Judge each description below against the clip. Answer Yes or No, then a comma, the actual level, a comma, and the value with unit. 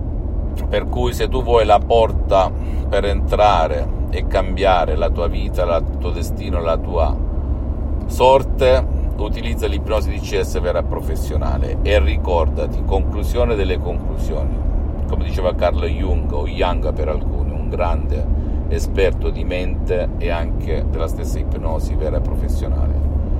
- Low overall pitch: Yes, very low, 75 Hz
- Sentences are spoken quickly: No, average, 130 wpm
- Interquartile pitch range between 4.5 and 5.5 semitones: No, narrow, 2.4 semitones